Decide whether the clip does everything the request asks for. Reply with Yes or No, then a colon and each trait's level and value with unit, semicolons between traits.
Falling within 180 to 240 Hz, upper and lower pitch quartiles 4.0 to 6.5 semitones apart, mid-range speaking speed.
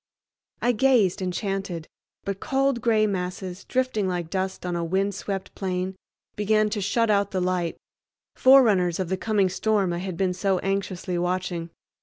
No: high, 190 Hz; average, 2.7 semitones; average, 160 wpm